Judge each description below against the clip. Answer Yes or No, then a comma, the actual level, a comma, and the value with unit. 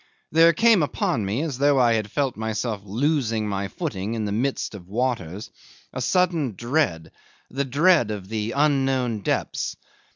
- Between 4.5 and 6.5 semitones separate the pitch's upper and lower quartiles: Yes, average, 5.3 semitones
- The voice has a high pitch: No, low, 120 Hz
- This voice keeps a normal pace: Yes, average, 160 wpm